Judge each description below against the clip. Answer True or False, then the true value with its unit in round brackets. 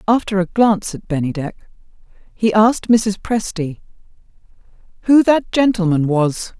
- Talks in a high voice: True (200 Hz)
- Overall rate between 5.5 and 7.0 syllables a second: False (4.9 syllables/s)